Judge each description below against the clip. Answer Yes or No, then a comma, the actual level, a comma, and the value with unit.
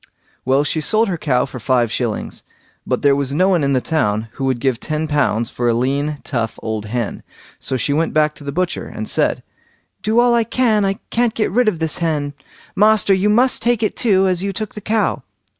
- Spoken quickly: Yes, fast, 225 wpm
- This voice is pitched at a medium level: Yes, medium, 155 Hz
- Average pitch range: No, wide, 8.0 semitones